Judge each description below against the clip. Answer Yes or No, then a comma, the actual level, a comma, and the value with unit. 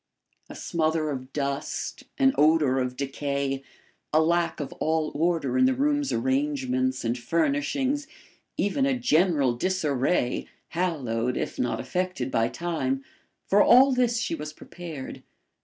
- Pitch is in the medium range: Yes, medium, 160 Hz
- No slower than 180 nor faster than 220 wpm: No, slow, 135 wpm